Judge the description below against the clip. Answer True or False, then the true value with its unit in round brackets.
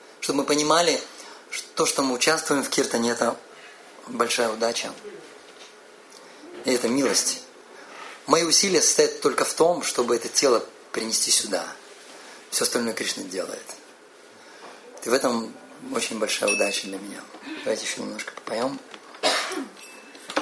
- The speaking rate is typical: True (125 wpm)